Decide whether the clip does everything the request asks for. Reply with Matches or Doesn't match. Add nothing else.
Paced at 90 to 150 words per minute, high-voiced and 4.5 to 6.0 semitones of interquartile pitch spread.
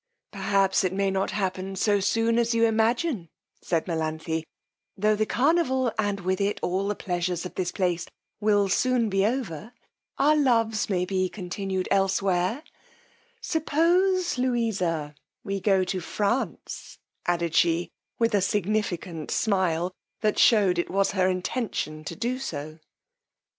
Doesn't match